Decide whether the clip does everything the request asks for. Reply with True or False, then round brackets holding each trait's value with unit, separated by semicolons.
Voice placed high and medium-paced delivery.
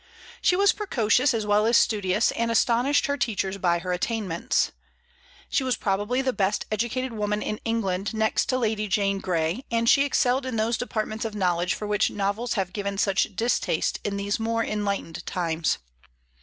True (215 Hz; 175 wpm)